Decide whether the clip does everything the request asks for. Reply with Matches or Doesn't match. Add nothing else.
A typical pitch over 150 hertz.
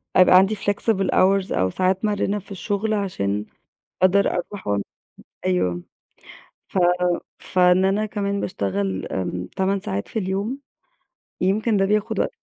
Matches